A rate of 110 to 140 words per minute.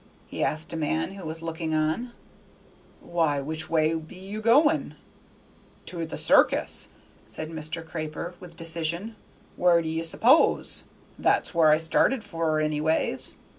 Yes: slow, 135 wpm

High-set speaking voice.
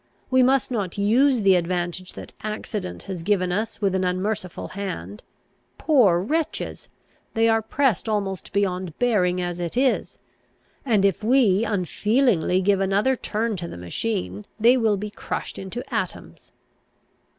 Yes: high, 200 Hz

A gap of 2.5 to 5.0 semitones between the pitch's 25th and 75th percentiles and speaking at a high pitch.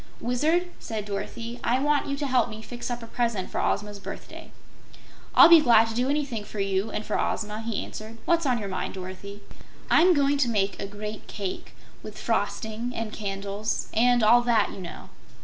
Yes: average, 3.1 semitones; high, 225 Hz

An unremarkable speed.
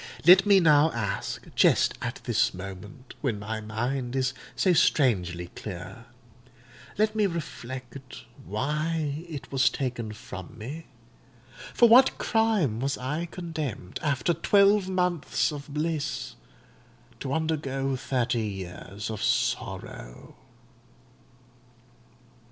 No: slow, 105 wpm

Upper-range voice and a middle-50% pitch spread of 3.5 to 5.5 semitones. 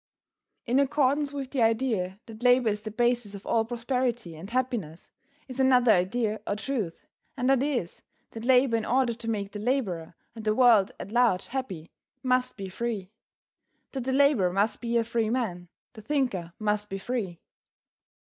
Yes: high, 230 Hz; average, 4.0 semitones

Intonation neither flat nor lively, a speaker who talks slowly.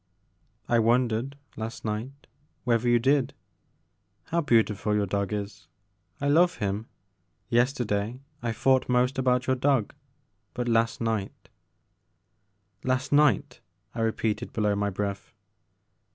Yes: average, 3.6 semitones; slow, 125 wpm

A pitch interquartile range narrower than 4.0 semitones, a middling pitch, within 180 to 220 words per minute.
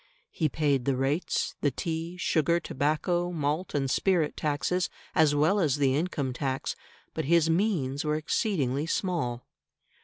No: average, 3.6 semitones; medium, 155 Hz; average, 145 wpm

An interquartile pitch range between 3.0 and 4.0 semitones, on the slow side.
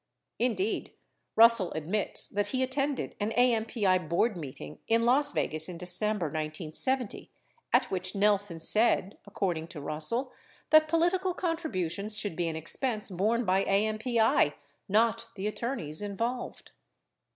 No: average, 5.2 semitones; slow, 130 wpm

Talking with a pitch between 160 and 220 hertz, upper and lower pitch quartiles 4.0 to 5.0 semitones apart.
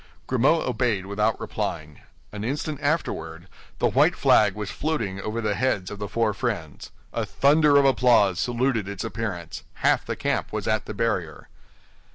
No: low, 110 Hz; average, 4.6 semitones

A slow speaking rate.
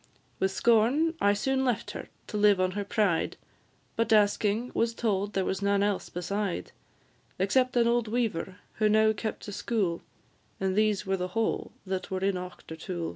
No: average, 175 wpm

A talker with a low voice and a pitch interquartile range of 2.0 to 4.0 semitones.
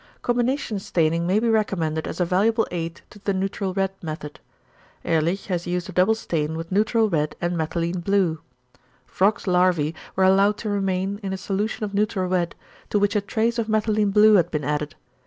No: high, 190 Hz; average, 3.6 semitones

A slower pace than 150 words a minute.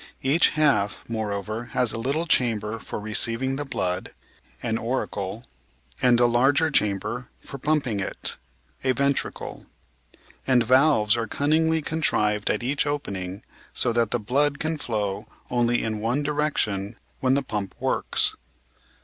Yes: average, 140 wpm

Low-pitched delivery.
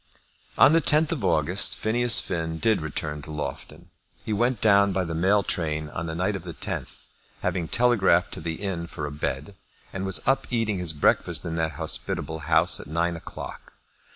Yes: very low, 90 Hz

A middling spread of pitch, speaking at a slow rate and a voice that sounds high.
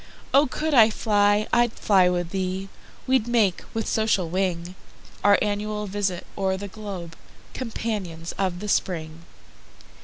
Yes: average, 3.0 semitones; slow, 120 wpm; high, 200 Hz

